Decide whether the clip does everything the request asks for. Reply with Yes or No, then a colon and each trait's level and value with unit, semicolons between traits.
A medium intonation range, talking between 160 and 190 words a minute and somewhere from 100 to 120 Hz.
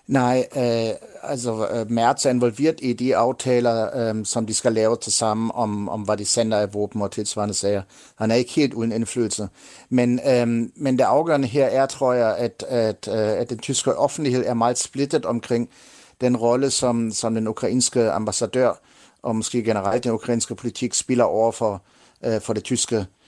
No: narrow, 2.1 semitones; average, 185 wpm; low, 115 Hz